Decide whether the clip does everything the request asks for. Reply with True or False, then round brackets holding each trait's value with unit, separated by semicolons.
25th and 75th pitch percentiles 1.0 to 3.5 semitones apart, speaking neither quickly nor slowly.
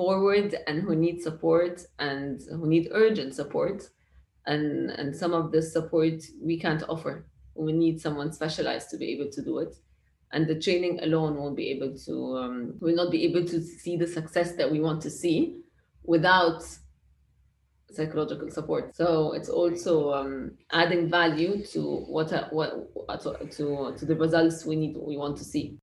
True (2.7 semitones; 170 wpm)